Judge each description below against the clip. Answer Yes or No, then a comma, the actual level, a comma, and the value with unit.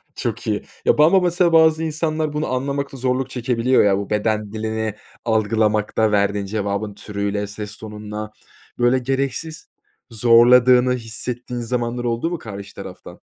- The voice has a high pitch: No, low, 120 Hz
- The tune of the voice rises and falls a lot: No, average, 3.9 semitones